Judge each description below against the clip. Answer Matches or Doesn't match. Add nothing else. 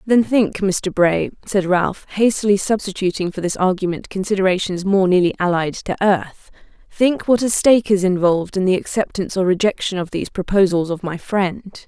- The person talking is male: Doesn't match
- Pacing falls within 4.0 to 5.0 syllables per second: Doesn't match